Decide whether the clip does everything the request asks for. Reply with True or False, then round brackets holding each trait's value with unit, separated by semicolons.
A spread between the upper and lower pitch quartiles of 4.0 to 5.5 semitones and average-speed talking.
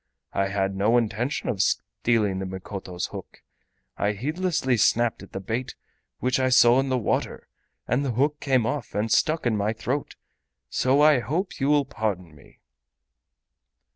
True (5.0 semitones; 165 wpm)